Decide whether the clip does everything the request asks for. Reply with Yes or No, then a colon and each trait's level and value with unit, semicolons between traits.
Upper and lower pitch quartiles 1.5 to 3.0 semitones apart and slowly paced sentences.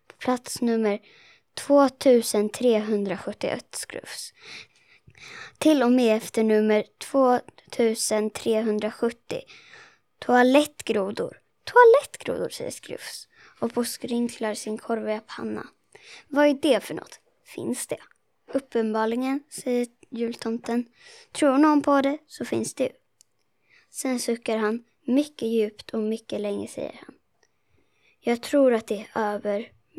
No: average, 4.3 semitones; slow, 105 wpm